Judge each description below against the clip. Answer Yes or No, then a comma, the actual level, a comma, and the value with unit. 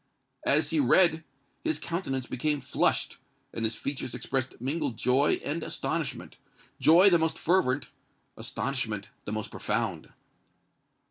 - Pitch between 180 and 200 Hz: No, medium, 140 Hz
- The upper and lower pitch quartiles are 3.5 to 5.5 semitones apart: Yes, average, 5.1 semitones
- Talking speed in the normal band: No, slow, 120 wpm